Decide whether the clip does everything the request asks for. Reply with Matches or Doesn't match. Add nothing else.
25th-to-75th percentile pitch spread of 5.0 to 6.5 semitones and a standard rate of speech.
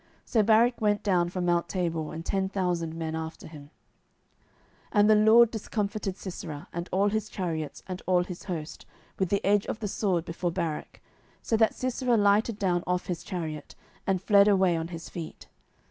Doesn't match